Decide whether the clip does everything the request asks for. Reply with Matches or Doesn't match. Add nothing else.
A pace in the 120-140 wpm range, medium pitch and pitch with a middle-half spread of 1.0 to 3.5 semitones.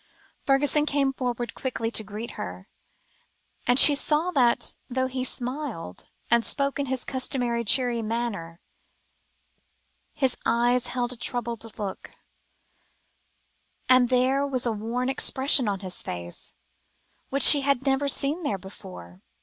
Doesn't match